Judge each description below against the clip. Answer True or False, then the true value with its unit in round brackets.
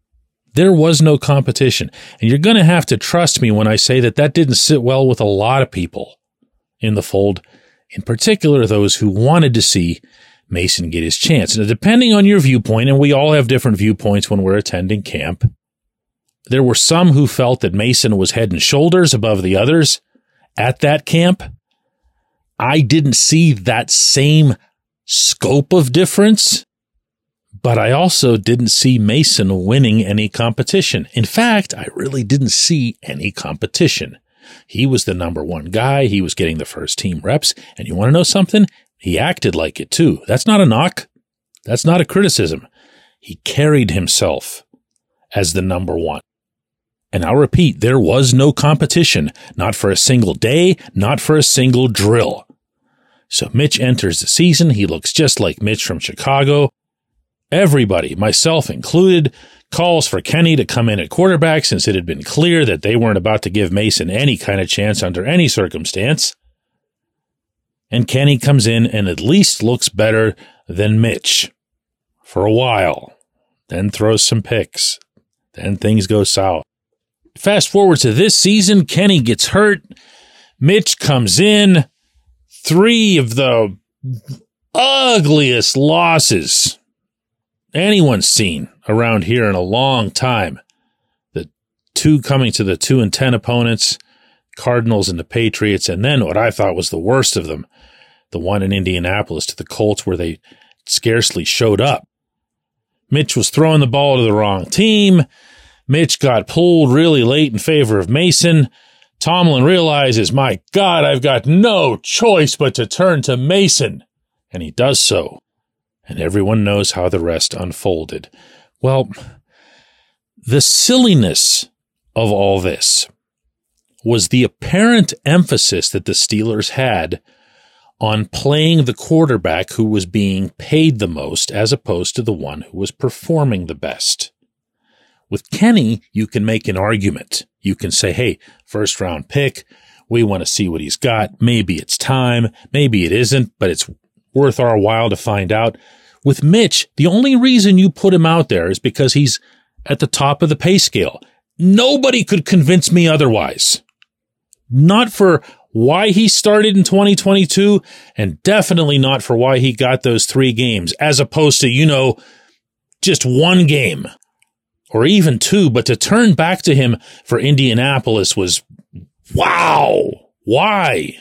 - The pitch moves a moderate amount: False (6.8 semitones)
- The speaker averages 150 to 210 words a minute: True (160 wpm)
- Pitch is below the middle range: True (130 Hz)